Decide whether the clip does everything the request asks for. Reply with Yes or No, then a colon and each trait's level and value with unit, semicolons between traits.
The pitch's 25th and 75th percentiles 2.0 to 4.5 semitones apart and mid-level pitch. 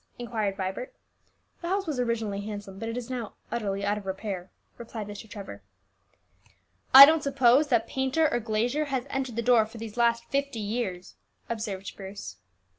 No: average, 3.8 semitones; high, 230 Hz